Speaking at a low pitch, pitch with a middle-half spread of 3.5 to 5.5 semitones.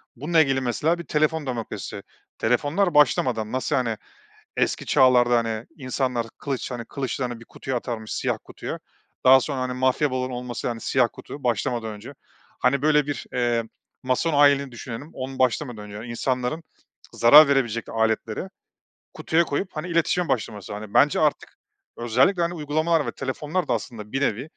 Yes: low, 130 Hz; average, 3.8 semitones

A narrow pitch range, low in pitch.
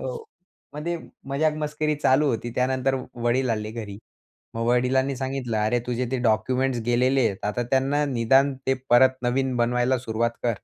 Yes: narrow, 2.2 semitones; low, 130 Hz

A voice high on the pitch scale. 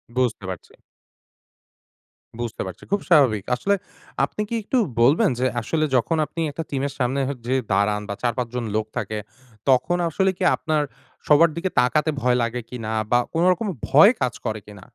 No: low, 130 Hz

